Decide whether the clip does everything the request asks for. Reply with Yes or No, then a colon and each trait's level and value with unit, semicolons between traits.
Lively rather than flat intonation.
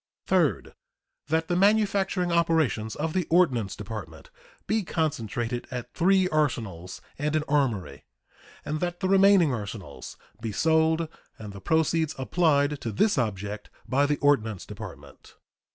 Yes: wide, 7.1 semitones